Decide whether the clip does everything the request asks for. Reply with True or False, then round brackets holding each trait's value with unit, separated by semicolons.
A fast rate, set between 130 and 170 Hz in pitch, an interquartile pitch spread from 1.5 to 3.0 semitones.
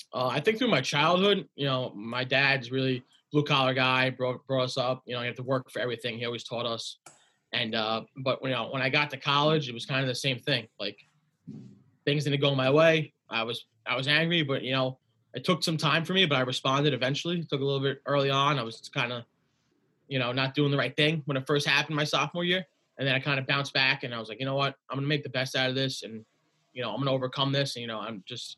True (275 wpm; 135 Hz; 2.5 semitones)